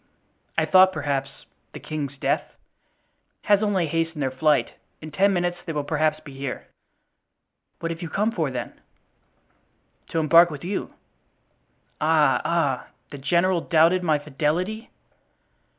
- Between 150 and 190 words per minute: No, average, 140 wpm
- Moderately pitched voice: Yes, medium, 160 Hz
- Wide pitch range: No, average, 3.3 semitones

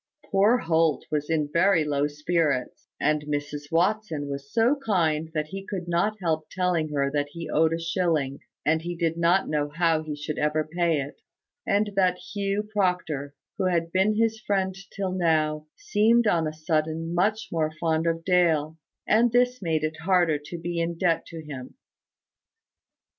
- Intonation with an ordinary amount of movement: Yes, average, 3.5 semitones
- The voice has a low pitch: No, medium, 165 Hz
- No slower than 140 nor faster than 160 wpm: No, average, 175 wpm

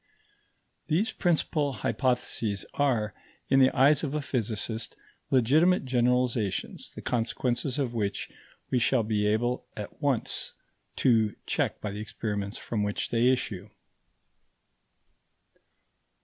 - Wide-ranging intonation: No, average, 3.9 semitones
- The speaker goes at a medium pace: No, slow, 115 wpm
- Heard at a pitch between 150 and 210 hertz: No, low, 120 Hz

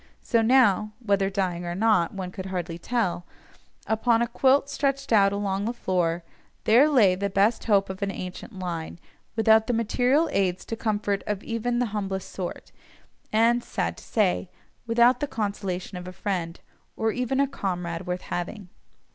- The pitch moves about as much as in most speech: Yes, average, 4.1 semitones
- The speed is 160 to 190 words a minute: Yes, average, 170 wpm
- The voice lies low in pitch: No, high, 205 Hz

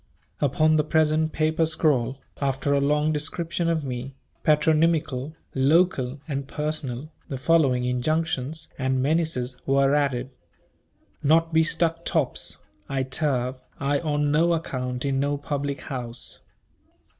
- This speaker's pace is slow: Yes, slow, 125 wpm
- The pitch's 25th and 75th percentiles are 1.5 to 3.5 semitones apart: Yes, average, 3.1 semitones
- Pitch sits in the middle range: Yes, medium, 145 Hz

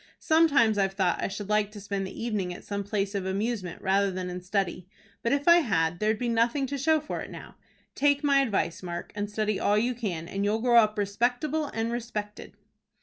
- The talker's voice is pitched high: Yes, high, 210 Hz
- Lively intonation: No, average, 3.7 semitones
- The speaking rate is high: Yes, fast, 215 wpm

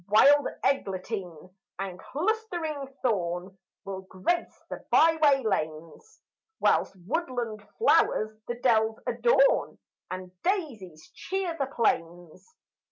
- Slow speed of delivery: Yes, slow, 100 wpm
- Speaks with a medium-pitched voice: No, high, 225 Hz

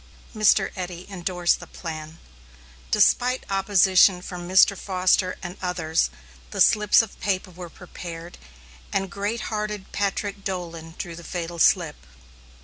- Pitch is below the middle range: No, medium, 185 Hz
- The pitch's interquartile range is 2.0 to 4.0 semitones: Yes, narrow, 2.4 semitones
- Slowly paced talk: Yes, slow, 130 wpm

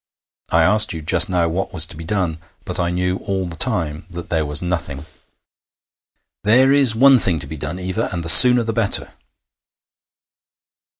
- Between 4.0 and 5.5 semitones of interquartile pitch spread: Yes, average, 4.6 semitones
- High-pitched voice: No, very low, 90 Hz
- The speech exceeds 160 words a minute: Yes, average, 180 wpm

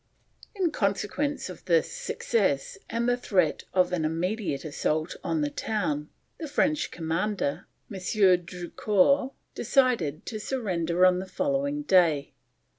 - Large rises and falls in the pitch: Yes, wide, 7.7 semitones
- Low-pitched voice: No, high, 190 Hz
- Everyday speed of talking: No, slow, 125 wpm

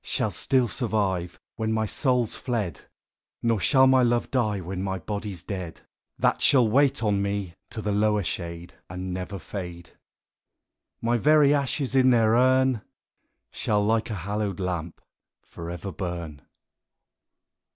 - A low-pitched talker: Yes, low, 105 Hz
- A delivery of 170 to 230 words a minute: No, average, 140 wpm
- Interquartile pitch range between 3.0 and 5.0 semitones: Yes, average, 4.7 semitones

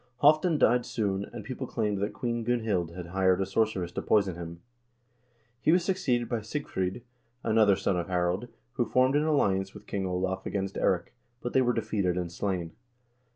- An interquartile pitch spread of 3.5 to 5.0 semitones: Yes, average, 4.7 semitones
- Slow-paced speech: No, average, 180 wpm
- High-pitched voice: No, low, 105 Hz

